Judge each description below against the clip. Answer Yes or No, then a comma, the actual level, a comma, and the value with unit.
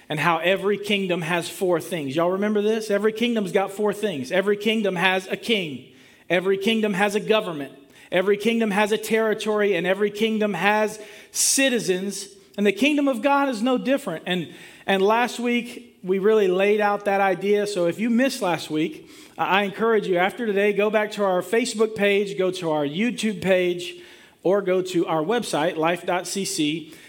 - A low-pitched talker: No, high, 200 Hz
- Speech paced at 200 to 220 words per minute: No, average, 180 wpm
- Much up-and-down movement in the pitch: No, average, 3.3 semitones